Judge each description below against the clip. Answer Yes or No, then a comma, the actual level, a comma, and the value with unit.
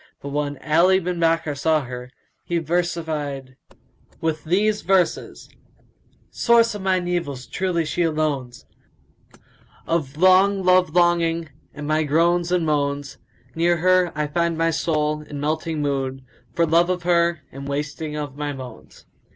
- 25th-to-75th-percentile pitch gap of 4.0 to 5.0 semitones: No, average, 3.0 semitones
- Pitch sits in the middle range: Yes, medium, 160 Hz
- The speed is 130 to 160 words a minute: Yes, average, 150 wpm